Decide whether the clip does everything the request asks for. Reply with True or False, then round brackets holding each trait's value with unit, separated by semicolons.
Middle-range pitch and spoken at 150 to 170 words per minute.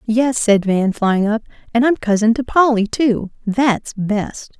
False (225 Hz; 155 wpm)